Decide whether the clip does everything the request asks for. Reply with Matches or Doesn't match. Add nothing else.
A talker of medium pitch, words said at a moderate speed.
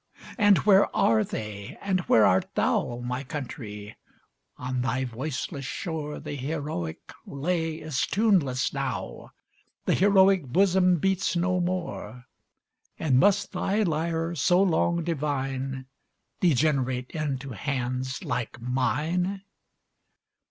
Doesn't match